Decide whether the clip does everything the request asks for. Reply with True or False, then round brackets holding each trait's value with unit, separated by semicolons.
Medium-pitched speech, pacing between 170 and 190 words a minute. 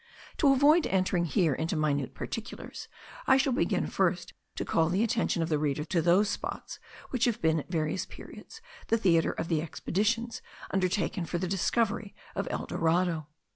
True (180 Hz; 175 wpm)